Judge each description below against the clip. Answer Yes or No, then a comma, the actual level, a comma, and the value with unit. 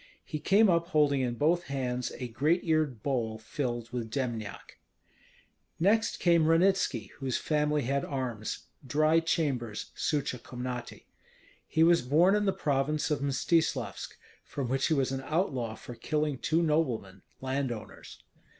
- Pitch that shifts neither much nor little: Yes, average, 4.5 semitones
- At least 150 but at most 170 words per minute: No, average, 140 wpm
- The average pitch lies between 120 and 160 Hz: Yes, medium, 140 Hz